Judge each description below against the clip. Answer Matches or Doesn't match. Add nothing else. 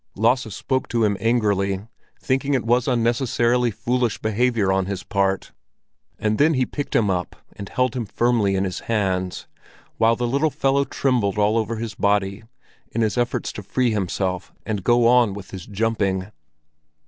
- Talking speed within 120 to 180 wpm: Matches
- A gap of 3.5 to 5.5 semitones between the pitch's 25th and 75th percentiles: Matches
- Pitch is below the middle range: Matches